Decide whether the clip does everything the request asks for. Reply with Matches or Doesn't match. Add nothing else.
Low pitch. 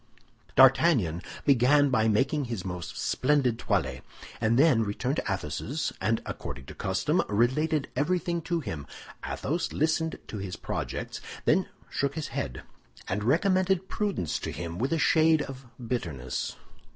Matches